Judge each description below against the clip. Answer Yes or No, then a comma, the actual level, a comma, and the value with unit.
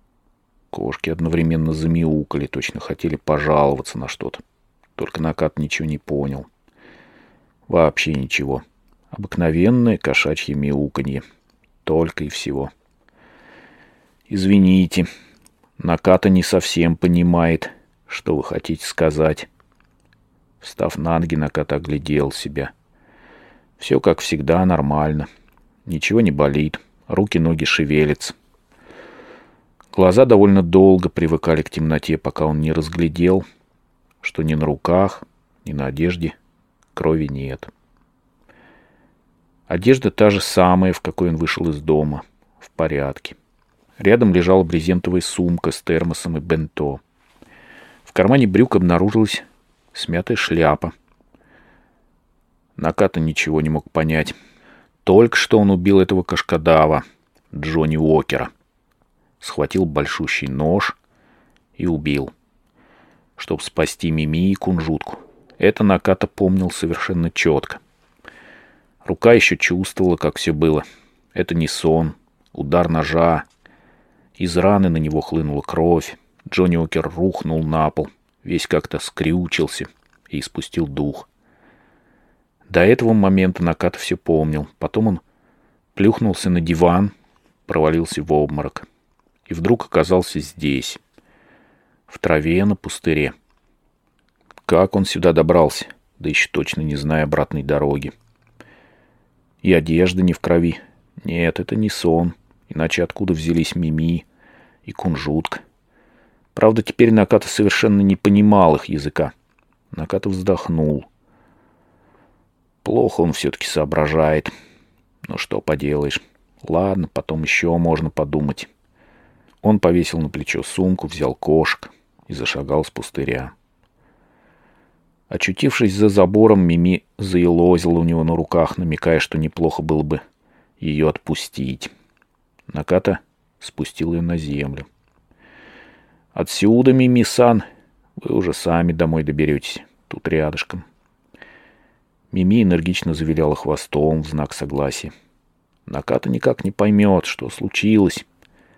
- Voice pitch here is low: Yes, very low, 80 Hz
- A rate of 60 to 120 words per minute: Yes, slow, 110 wpm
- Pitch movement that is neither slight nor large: Yes, average, 3.2 semitones